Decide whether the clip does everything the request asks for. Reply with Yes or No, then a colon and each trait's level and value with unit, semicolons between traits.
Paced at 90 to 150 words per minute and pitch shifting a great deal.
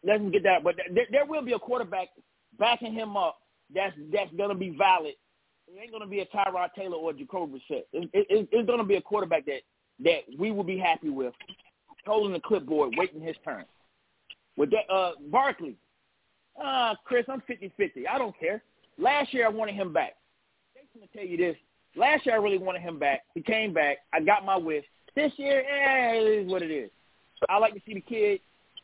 No: fast, 205 wpm; wide, 6.3 semitones